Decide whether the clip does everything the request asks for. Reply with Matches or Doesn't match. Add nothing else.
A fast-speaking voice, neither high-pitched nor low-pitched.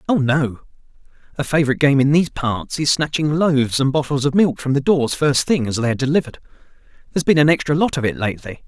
Matches